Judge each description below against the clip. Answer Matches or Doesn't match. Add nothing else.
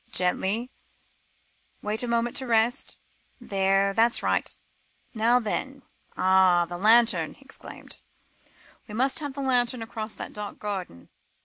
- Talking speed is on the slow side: Matches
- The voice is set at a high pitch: Matches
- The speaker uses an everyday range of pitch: Matches